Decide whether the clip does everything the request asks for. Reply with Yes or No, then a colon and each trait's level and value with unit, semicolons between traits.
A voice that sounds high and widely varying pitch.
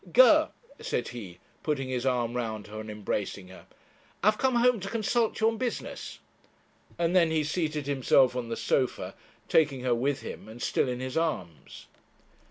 No: low, 135 Hz; wide, 6.4 semitones